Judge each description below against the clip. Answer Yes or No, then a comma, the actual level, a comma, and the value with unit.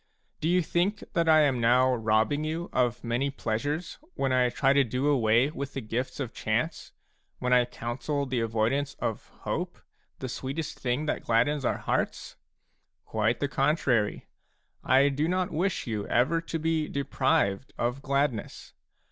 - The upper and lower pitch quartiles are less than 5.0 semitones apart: Yes, average, 4.0 semitones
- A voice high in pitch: No, low, 135 Hz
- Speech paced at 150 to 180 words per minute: Yes, average, 160 wpm